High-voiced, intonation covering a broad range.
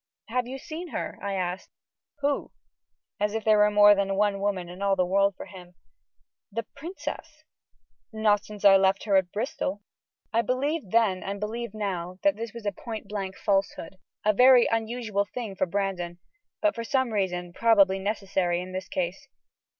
No: high, 205 Hz; average, 3.2 semitones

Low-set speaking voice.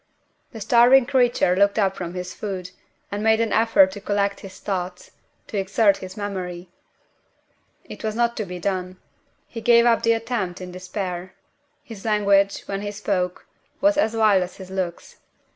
No: high, 200 Hz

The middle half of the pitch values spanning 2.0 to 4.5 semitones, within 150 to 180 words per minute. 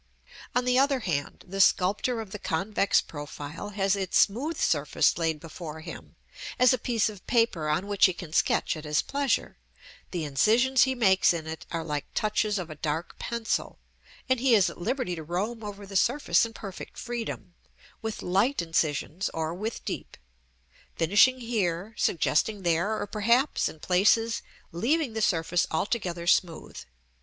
No: wide, 5.6 semitones; average, 165 wpm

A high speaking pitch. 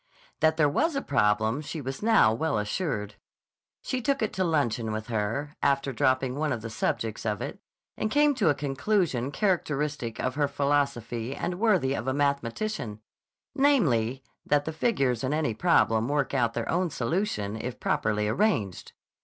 No: medium, 140 Hz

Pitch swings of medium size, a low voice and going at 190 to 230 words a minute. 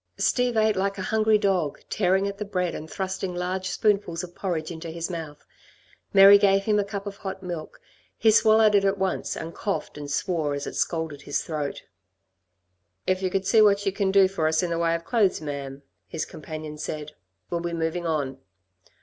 No: average, 3.7 semitones; medium, 185 Hz; average, 200 wpm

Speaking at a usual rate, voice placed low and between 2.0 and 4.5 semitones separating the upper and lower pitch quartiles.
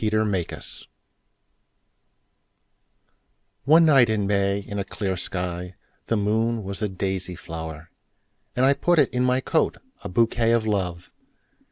No: slow, 120 wpm; low, 105 Hz; average, 3.9 semitones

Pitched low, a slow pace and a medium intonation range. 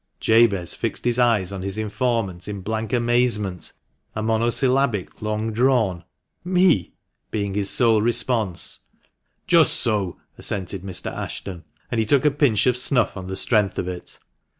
No: low, 110 Hz; average, 165 wpm; average, 3.7 semitones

